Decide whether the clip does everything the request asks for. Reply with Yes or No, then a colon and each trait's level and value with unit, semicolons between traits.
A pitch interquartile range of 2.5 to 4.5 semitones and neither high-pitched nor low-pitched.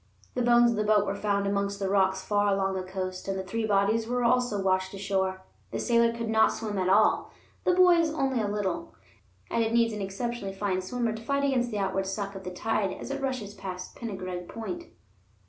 No: average, 3.3 semitones; high, 205 Hz